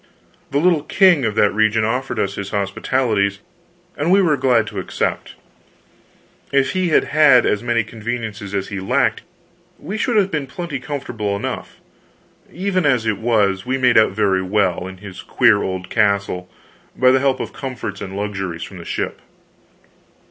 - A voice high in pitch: No, low, 110 Hz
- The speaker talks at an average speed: Yes, average, 170 wpm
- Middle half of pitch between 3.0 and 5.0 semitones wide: No, wide, 5.5 semitones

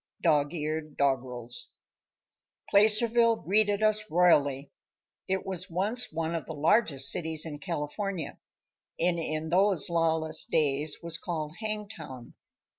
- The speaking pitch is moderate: Yes, medium, 165 Hz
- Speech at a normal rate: No, slow, 115 wpm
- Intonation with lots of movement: No, average, 4.8 semitones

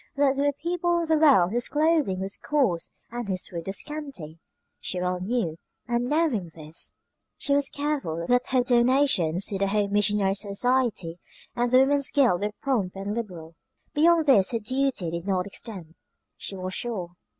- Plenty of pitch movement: Yes, wide, 6.9 semitones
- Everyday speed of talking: Yes, average, 175 wpm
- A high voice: Yes, high, 230 Hz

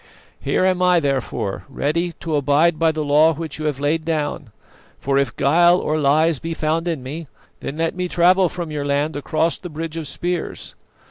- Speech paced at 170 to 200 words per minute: Yes, average, 195 wpm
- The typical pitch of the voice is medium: Yes, medium, 155 Hz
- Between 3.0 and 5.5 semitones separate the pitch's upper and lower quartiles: No, narrow, 2.6 semitones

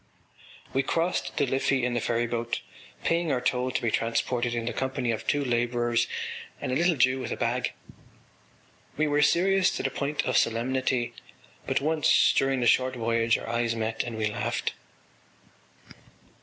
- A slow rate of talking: No, average, 170 wpm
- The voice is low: Yes, low, 125 Hz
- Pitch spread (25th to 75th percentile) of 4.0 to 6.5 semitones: No, narrow, 2.6 semitones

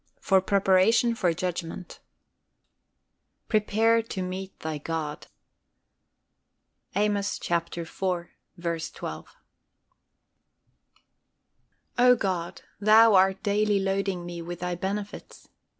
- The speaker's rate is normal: No, slow, 85 wpm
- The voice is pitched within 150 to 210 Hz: Yes, high, 190 Hz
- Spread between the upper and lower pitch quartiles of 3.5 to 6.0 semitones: No, average, 3.1 semitones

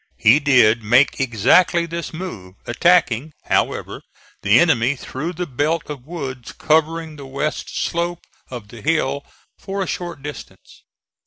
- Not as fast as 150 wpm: Yes, average, 140 wpm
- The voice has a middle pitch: Yes, medium, 145 Hz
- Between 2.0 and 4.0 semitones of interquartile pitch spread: No, average, 5.0 semitones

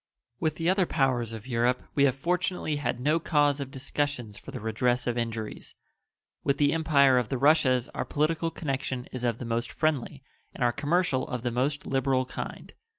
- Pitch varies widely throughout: No, average, 3.3 semitones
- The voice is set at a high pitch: No, low, 135 Hz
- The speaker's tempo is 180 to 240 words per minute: Yes, average, 190 wpm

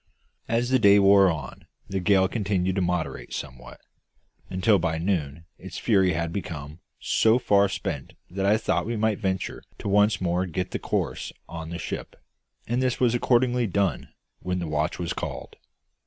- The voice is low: Yes, very low, 95 Hz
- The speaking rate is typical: Yes, average, 170 wpm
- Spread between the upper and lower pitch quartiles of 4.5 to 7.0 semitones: No, average, 3.7 semitones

